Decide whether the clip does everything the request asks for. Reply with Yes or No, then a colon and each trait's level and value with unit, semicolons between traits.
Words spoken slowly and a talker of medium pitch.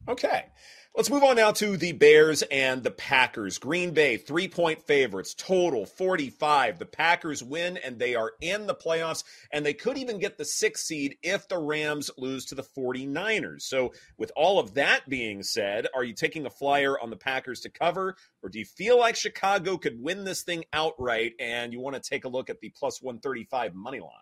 No: fast, 205 wpm; medium, 155 Hz